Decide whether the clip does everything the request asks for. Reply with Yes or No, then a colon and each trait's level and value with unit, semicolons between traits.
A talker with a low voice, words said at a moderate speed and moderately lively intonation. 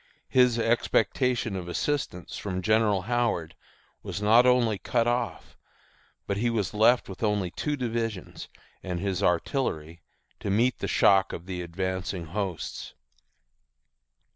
No: low, 105 Hz; slow, 130 wpm; average, 4.4 semitones